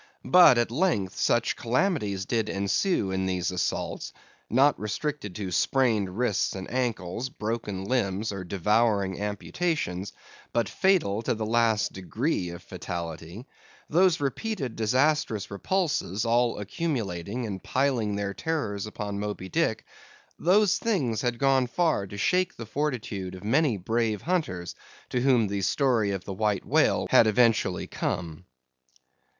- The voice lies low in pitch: Yes, low, 110 Hz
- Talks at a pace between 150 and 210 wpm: No, slow, 135 wpm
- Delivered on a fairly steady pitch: No, average, 5.2 semitones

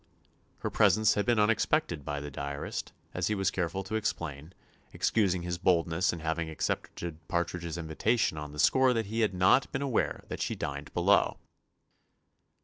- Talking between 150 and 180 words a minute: Yes, average, 165 wpm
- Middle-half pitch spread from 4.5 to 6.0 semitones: Yes, average, 5.1 semitones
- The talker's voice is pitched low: Yes, very low, 90 Hz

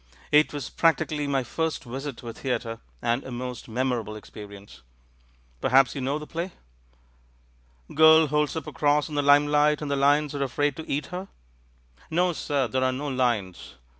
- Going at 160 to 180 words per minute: Yes, average, 175 wpm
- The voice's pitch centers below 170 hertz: Yes, medium, 140 Hz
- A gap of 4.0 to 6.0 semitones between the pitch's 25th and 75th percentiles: No, average, 3.0 semitones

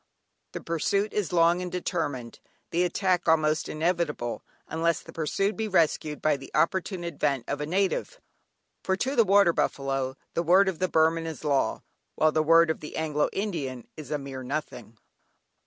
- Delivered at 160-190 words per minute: Yes, average, 170 wpm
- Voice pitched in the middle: Yes, medium, 165 Hz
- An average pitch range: Yes, average, 3.4 semitones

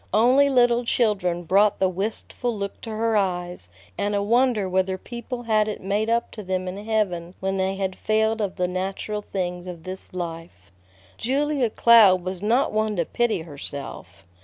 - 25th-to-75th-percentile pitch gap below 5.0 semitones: Yes, average, 3.5 semitones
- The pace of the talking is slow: No, average, 175 wpm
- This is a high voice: Yes, high, 200 Hz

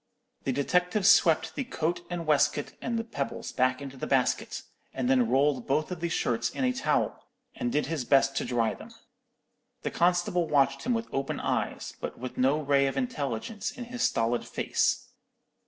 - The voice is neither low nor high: Yes, medium, 145 Hz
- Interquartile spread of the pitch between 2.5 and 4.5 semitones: No, average, 5.2 semitones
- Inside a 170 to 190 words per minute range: Yes, average, 185 wpm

